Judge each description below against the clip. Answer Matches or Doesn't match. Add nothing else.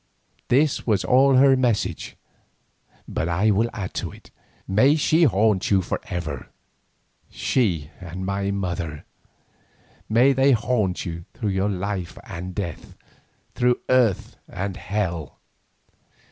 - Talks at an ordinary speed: Doesn't match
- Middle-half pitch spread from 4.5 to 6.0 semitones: Matches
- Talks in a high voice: Doesn't match